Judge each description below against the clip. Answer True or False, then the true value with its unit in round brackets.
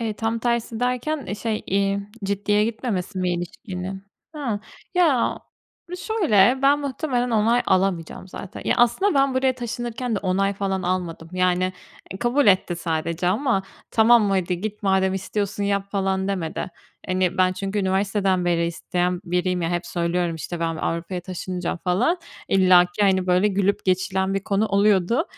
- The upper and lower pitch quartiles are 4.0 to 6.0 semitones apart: False (3.6 semitones)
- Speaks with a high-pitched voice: True (195 Hz)